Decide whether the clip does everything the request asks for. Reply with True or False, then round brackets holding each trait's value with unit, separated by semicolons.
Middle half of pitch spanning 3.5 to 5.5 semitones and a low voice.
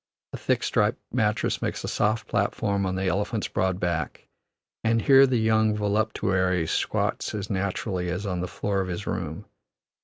False (2.8 semitones; 100 Hz)